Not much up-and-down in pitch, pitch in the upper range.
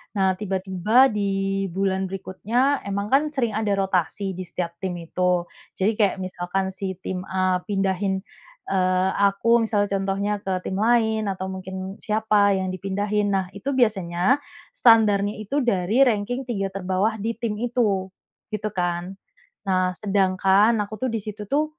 Yes: narrow, 2.3 semitones; high, 195 Hz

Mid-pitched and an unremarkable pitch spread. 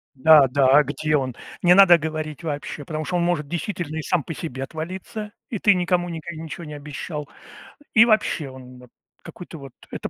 Yes: medium, 155 Hz; average, 3.4 semitones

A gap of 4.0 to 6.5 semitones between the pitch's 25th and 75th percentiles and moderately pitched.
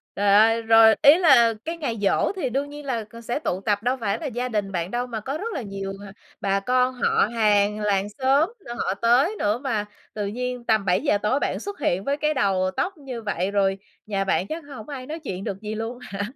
No: average, 4.7 semitones; high, 225 Hz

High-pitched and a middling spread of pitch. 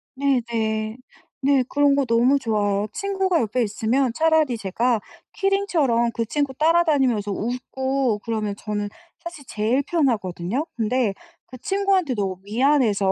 Yes: very high, 250 Hz; average, 4.9 semitones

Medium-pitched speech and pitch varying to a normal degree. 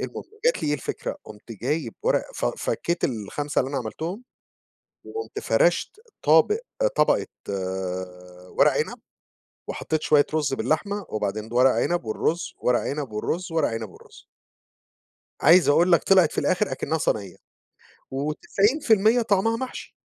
No: medium, 155 Hz; wide, 7.8 semitones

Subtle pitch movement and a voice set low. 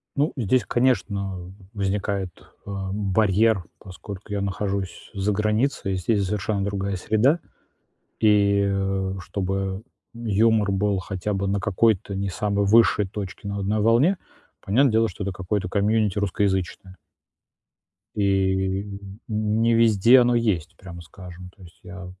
Yes: narrow, 2.1 semitones; low, 100 Hz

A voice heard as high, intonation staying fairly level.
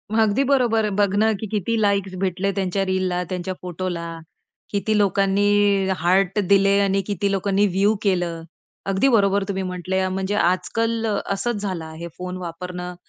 Yes: high, 195 Hz; narrow, 2.1 semitones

